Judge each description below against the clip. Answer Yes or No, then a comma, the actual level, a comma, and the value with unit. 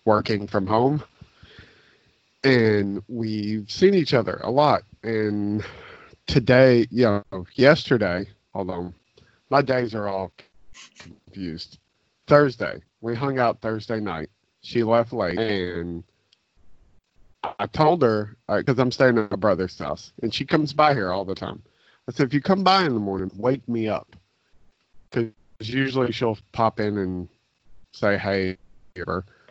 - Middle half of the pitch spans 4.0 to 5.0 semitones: Yes, average, 4.5 semitones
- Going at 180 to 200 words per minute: No, average, 140 wpm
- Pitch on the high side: No, low, 110 Hz